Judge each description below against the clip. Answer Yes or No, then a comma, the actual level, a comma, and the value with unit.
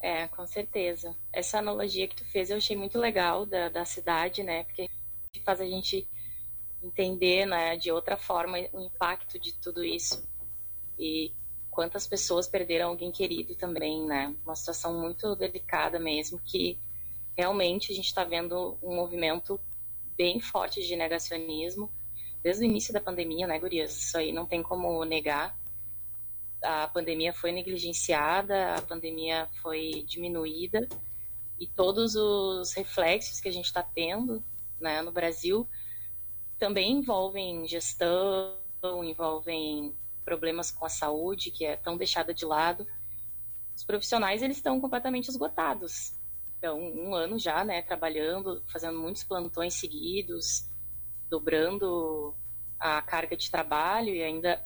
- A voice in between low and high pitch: Yes, medium, 170 Hz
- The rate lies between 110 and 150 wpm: Yes, average, 135 wpm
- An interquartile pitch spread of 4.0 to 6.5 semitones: No, average, 3.3 semitones